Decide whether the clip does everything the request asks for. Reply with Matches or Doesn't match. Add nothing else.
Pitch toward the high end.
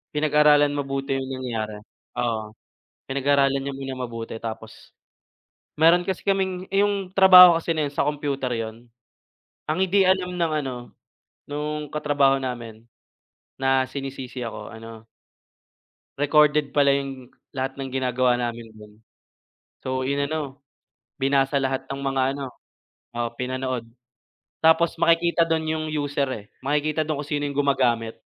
Doesn't match